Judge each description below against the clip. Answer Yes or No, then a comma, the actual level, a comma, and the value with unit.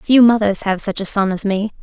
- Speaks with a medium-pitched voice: No, high, 205 Hz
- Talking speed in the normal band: No, fast, 265 wpm